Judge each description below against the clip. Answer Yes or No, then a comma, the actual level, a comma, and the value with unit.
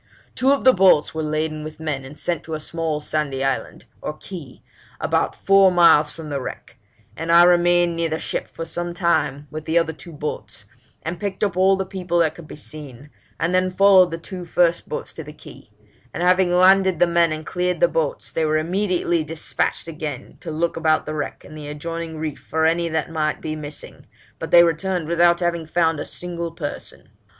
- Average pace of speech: No, fast, 210 wpm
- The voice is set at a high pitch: No, medium, 165 Hz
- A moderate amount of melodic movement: No, narrow, 2.3 semitones